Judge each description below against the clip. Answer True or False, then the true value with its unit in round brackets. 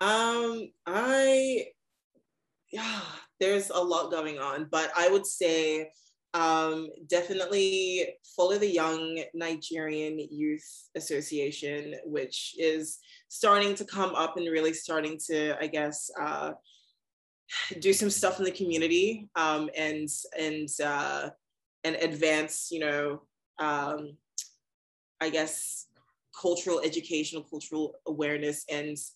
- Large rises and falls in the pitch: False (3.4 semitones)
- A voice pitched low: False (160 Hz)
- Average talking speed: False (115 wpm)